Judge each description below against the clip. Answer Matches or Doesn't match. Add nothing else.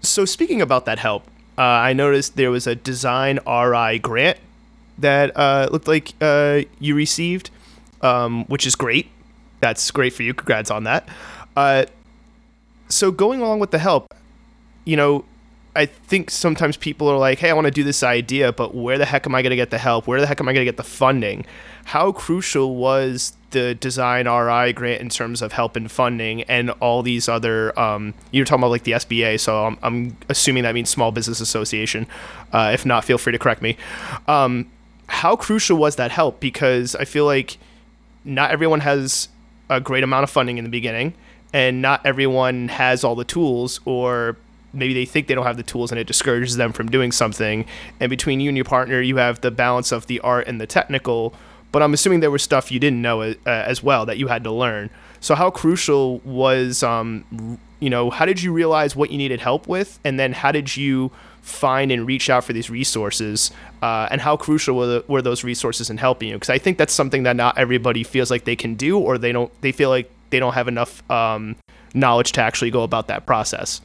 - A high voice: Doesn't match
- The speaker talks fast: Matches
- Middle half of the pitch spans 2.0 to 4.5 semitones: Matches